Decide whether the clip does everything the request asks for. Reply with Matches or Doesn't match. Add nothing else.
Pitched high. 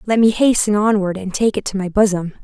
Matches